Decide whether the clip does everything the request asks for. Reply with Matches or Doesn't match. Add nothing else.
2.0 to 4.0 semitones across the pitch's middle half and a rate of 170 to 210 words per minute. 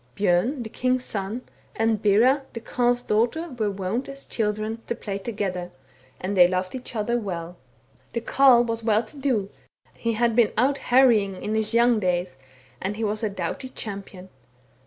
Matches